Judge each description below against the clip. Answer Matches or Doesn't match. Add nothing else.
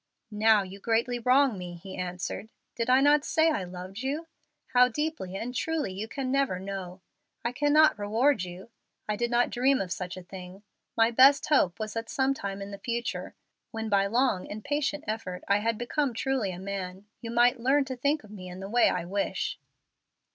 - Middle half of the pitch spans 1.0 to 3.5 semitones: Doesn't match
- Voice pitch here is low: Doesn't match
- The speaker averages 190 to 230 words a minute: Matches